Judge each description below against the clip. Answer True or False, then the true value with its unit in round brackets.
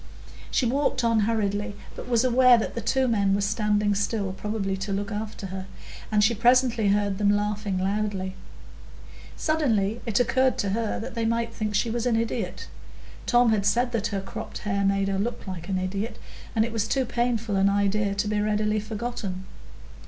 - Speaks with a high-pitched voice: True (210 Hz)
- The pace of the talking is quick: False (190 wpm)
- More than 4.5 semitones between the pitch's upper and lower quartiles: False (2.6 semitones)